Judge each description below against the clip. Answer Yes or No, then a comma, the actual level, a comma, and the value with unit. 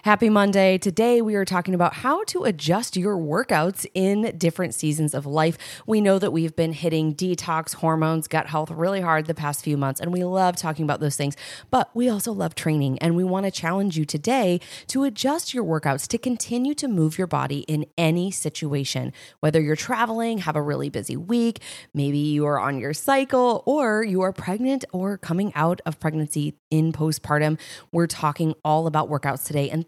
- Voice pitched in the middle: Yes, medium, 170 Hz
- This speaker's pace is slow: No, average, 195 wpm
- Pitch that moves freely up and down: No, average, 4.8 semitones